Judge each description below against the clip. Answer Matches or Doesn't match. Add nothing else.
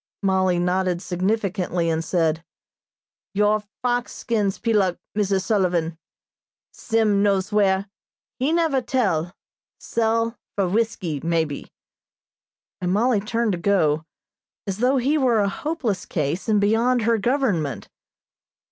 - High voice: Matches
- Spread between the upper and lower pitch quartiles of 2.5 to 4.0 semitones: Doesn't match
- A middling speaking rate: Doesn't match